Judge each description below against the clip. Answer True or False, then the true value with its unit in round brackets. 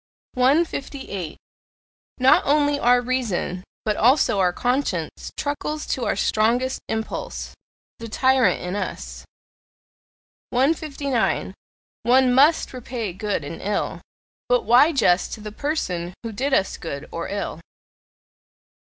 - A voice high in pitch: True (245 Hz)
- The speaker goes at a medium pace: False (115 wpm)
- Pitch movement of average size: False (5.8 semitones)